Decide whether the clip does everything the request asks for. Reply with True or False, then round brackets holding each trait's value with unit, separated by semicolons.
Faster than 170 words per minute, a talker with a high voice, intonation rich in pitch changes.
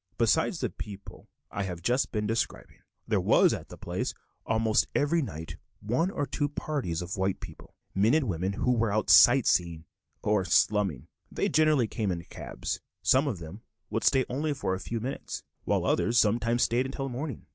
False (185 wpm; 115 Hz; 5.7 semitones)